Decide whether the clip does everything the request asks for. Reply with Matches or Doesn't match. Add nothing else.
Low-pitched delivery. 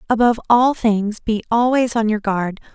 Doesn't match